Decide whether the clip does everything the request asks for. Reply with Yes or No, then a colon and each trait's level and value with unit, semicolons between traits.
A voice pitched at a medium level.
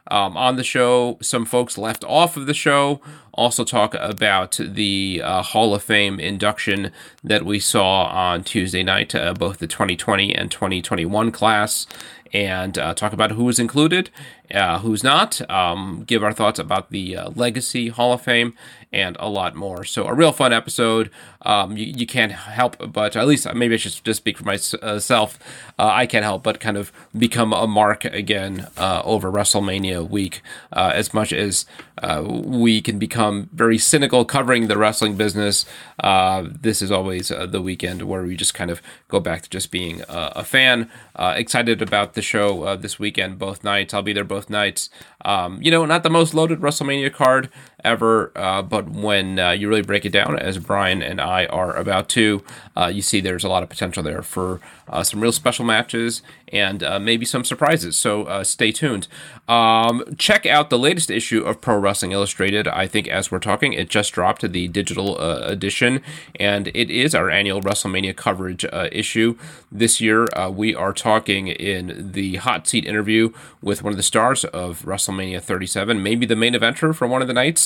No: low, 105 Hz